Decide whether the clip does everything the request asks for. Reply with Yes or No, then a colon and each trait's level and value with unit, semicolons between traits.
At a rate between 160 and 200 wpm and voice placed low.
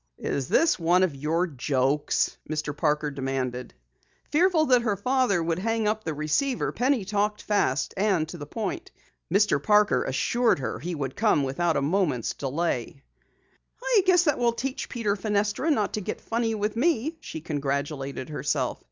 No: average, 165 wpm; medium, 185 Hz